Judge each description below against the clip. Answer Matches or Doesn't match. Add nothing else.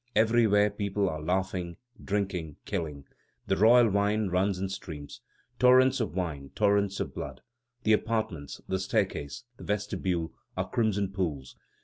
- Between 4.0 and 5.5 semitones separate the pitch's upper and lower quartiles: Doesn't match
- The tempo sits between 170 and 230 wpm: Doesn't match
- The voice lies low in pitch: Matches